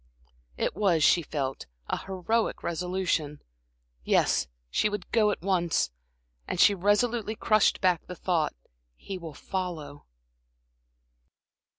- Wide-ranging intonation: No, average, 4.2 semitones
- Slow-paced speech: Yes, slow, 115 wpm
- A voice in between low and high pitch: Yes, medium, 180 Hz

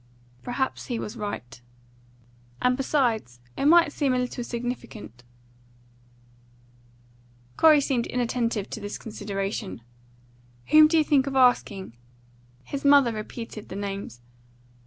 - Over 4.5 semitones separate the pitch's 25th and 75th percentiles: Yes, average, 4.9 semitones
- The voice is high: Yes, high, 240 Hz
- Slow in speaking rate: Yes, slow, 115 wpm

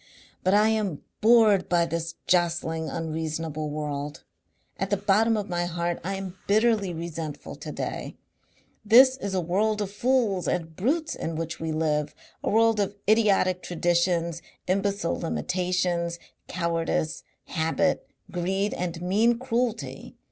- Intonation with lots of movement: No, average, 3.8 semitones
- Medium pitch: Yes, medium, 180 Hz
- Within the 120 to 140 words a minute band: Yes, slow, 135 wpm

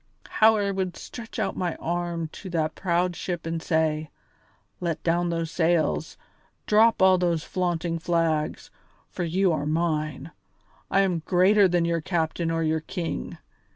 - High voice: No, medium, 170 Hz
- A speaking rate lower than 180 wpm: Yes, average, 155 wpm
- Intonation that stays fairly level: Yes, narrow, 2.0 semitones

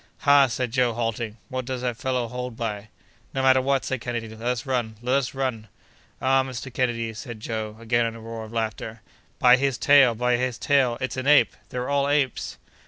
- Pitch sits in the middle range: No, low, 125 Hz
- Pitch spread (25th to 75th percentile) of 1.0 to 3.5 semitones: Yes, narrow, 2.5 semitones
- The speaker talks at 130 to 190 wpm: No, fast, 205 wpm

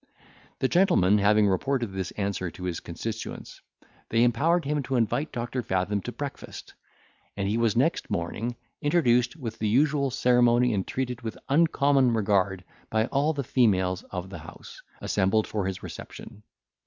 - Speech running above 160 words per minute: No, average, 155 wpm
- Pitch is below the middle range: Yes, low, 115 Hz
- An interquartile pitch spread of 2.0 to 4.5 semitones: No, average, 5.2 semitones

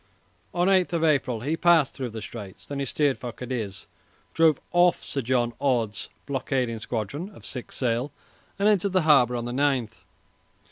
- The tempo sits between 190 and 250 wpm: No, average, 170 wpm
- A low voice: Yes, low, 130 Hz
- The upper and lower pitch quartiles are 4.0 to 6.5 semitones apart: Yes, average, 5.1 semitones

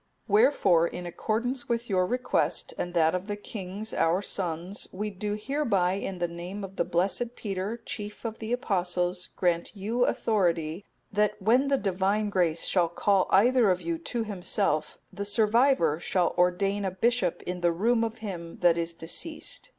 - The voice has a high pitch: Yes, high, 195 Hz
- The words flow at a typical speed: Yes, average, 170 wpm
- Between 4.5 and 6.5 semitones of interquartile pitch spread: No, average, 3.8 semitones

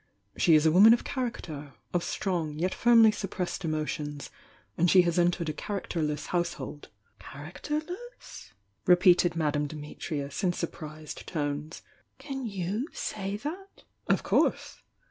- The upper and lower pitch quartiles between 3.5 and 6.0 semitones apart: Yes, average, 5.3 semitones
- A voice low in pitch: No, medium, 175 Hz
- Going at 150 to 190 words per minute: No, slow, 135 wpm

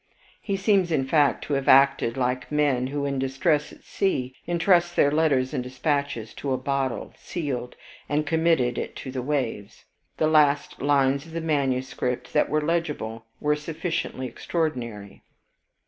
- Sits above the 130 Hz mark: Yes, medium, 140 Hz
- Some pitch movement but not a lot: Yes, average, 3.5 semitones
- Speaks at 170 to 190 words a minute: No, average, 155 wpm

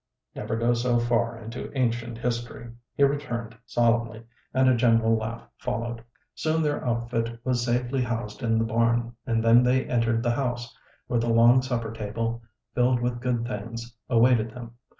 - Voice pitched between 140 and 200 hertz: No, low, 120 Hz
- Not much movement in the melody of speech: Yes, narrow, 1.1 semitones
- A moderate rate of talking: Yes, average, 165 wpm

